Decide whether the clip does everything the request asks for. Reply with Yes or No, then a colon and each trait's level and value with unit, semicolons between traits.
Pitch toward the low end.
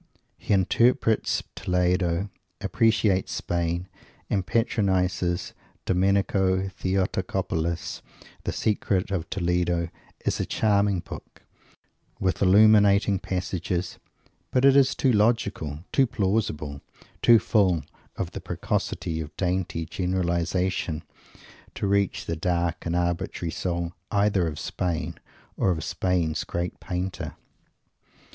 Yes: very low, 90 Hz